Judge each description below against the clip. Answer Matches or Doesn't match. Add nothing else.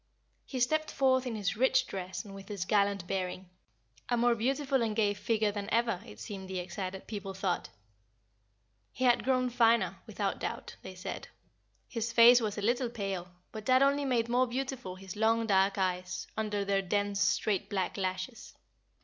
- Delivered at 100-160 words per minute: Doesn't match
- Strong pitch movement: Doesn't match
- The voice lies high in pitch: Matches